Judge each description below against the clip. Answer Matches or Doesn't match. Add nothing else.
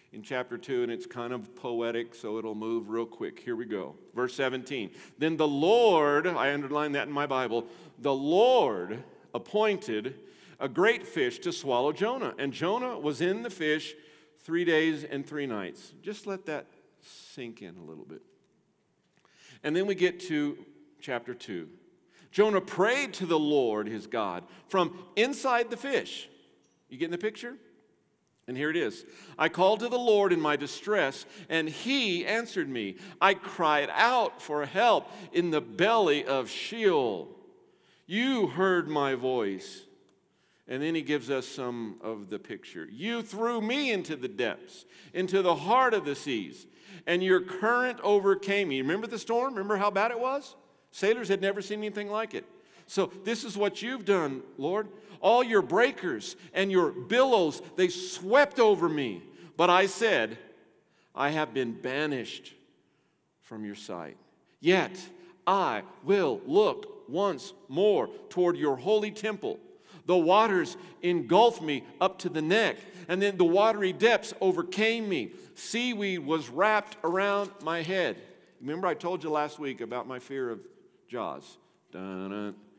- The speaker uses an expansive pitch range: Matches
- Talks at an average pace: Matches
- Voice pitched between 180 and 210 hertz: Matches